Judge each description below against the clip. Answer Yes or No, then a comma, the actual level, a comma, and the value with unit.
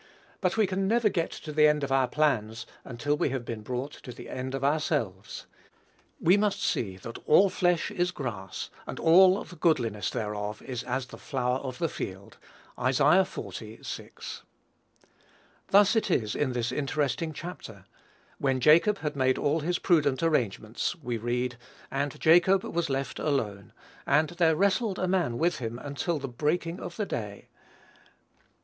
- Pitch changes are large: Yes, wide, 6.0 semitones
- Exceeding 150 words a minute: Yes, average, 165 wpm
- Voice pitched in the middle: Yes, medium, 145 Hz